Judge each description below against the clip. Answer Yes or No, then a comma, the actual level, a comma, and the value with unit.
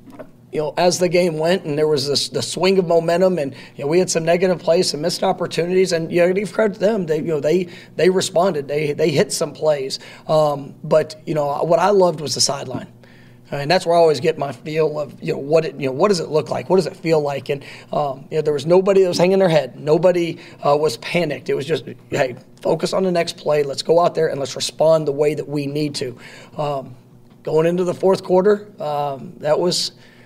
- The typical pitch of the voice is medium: Yes, medium, 165 Hz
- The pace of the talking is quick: Yes, fast, 260 wpm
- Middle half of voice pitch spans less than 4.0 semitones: Yes, average, 3.6 semitones